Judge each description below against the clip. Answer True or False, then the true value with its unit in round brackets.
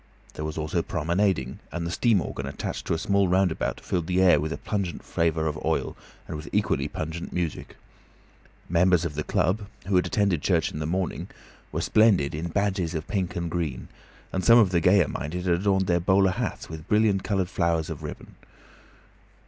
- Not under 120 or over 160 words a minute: False (195 wpm)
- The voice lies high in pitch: False (90 Hz)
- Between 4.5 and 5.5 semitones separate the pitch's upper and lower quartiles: False (3.1 semitones)